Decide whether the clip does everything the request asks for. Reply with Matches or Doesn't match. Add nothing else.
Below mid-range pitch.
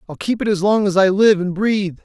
Doesn't match